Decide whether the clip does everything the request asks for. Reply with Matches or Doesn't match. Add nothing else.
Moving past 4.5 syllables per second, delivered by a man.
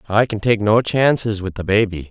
Matches